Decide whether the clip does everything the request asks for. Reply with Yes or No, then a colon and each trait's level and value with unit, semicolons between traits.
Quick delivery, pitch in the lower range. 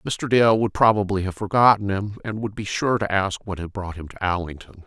Yes: fast, 235 wpm; low, 100 Hz